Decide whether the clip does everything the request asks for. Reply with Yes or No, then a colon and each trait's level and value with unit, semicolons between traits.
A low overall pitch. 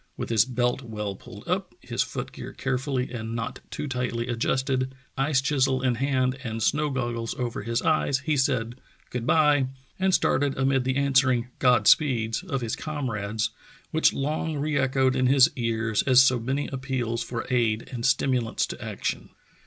Yes: low, 130 Hz